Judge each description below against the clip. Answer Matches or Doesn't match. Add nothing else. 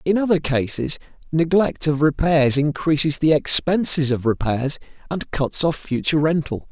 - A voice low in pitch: Doesn't match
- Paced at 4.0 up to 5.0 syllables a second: Matches